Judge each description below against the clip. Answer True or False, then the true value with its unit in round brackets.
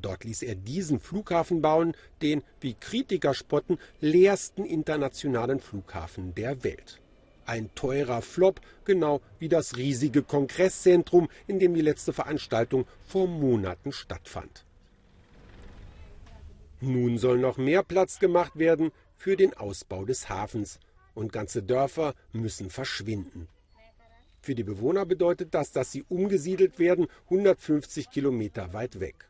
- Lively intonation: True (8.2 semitones)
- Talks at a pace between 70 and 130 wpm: True (125 wpm)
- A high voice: False (135 Hz)